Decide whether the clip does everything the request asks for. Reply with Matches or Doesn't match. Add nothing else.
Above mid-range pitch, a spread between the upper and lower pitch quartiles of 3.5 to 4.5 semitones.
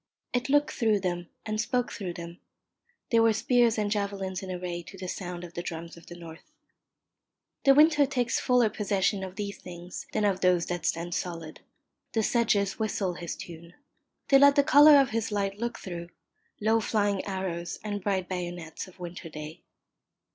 Matches